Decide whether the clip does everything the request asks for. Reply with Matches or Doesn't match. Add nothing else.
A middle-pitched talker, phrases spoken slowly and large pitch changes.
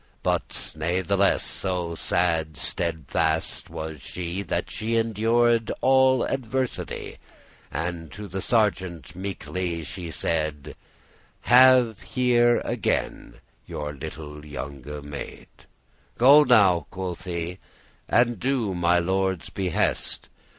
Doesn't match